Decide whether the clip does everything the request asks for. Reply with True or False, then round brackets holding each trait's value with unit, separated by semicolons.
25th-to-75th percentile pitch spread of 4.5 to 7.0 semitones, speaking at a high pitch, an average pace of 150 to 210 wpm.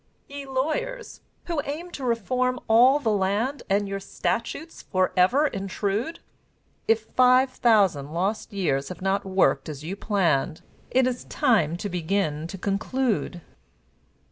False (5.5 semitones; 210 Hz; 135 wpm)